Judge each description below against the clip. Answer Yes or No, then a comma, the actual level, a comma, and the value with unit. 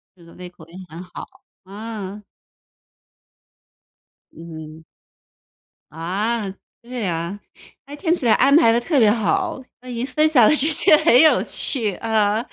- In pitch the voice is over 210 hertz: Yes, high, 220 Hz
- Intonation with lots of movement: Yes, wide, 5.8 semitones